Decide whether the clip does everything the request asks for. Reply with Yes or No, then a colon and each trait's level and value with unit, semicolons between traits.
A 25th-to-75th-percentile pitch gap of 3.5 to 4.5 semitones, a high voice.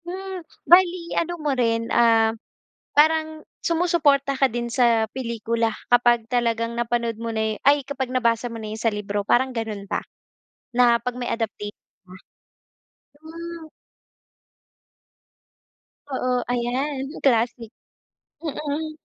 Yes: average, 4.2 semitones; high, 245 Hz